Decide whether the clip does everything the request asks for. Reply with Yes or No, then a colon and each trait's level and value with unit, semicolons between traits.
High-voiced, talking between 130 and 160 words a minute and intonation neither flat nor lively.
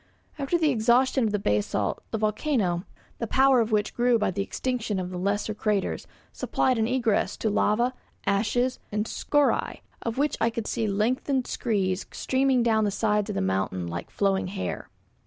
No: high, 220 Hz; average, 175 wpm; average, 3.9 semitones